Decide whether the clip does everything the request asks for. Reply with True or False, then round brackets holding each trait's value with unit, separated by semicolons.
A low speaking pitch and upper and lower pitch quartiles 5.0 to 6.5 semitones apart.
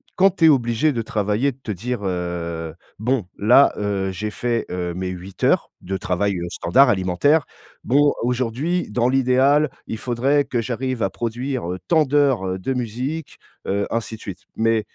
True (115 Hz; 5.6 semitones)